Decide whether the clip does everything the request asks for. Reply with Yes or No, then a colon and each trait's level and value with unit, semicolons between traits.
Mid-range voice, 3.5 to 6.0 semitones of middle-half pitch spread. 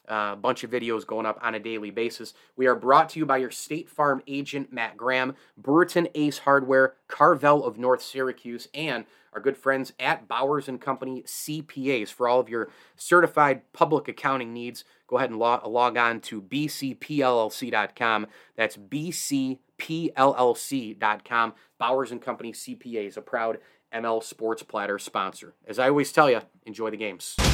No: low, 130 Hz; average, 3.8 semitones